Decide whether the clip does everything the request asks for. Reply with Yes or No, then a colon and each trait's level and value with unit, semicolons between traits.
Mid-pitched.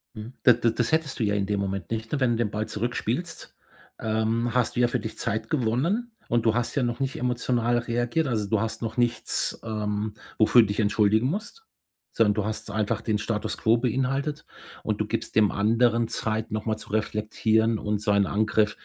No: low, 115 Hz